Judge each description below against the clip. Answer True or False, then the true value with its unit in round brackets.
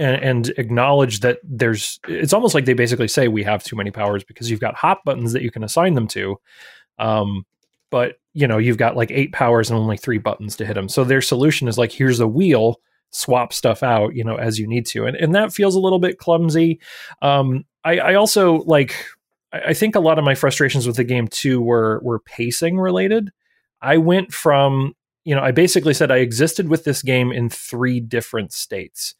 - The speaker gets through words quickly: True (215 wpm)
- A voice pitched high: False (130 Hz)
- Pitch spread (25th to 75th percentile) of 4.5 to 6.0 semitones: True (5.1 semitones)